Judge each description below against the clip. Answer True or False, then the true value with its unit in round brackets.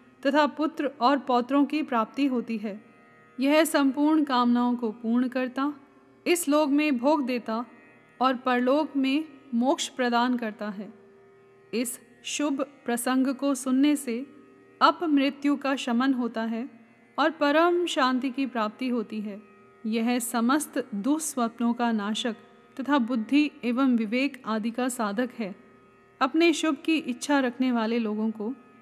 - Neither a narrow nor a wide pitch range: True (3.5 semitones)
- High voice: True (255 Hz)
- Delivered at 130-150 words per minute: True (135 wpm)